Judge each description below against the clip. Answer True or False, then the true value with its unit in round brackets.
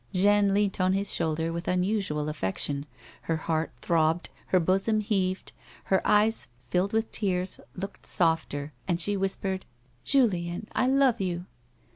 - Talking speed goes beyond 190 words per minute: False (145 wpm)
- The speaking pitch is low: False (185 Hz)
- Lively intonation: False (3.6 semitones)